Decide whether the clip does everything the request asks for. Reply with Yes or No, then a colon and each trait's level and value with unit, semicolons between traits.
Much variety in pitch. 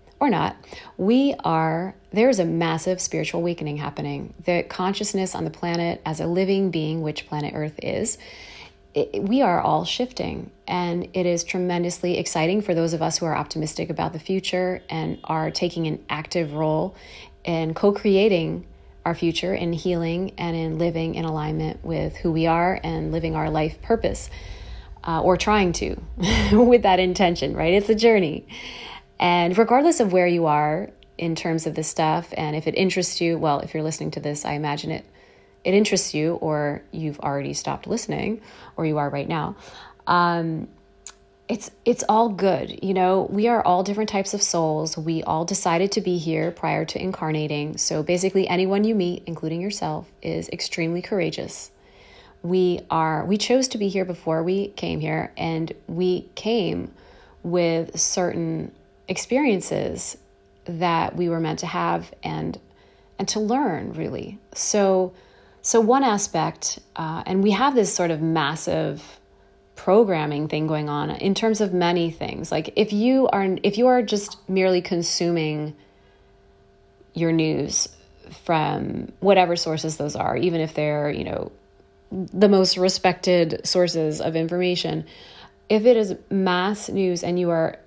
No: average, 3.4 semitones